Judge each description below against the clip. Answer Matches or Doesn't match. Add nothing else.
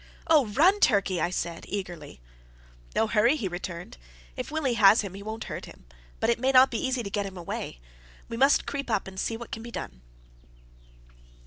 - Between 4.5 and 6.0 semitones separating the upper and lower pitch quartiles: Matches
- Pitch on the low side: Doesn't match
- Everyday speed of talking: Matches